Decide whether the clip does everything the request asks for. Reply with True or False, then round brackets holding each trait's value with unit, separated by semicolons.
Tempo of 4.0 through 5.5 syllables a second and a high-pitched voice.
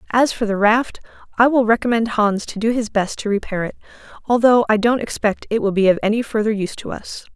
False (5.9 syllables/s; 220 Hz)